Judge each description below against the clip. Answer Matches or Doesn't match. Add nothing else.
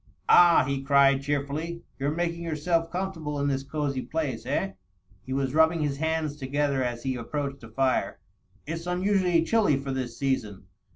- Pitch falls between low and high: Matches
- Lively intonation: Doesn't match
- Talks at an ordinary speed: Matches